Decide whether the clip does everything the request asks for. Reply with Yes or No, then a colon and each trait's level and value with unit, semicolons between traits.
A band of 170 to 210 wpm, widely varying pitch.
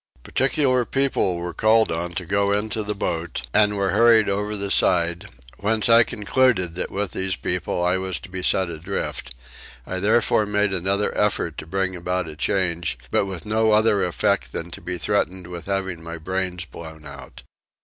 No: average, 180 wpm; average, 3.2 semitones